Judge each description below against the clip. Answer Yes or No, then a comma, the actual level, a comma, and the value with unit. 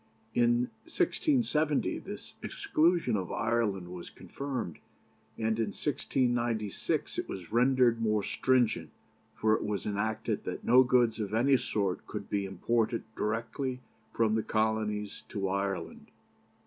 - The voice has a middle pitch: No, low, 115 Hz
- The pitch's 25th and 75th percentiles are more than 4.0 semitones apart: No, average, 3.4 semitones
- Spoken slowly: Yes, slow, 125 wpm